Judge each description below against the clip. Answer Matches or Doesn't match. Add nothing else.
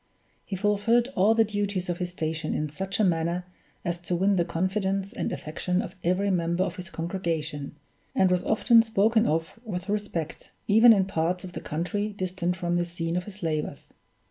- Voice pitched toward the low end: Doesn't match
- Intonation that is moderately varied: Matches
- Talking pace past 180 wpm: Matches